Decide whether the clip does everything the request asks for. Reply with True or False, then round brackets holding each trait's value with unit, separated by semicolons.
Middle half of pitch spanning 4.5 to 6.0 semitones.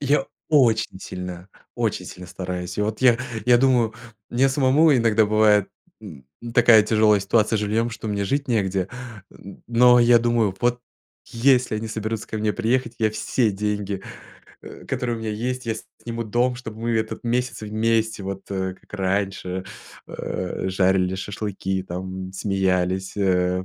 False (3.7 semitones)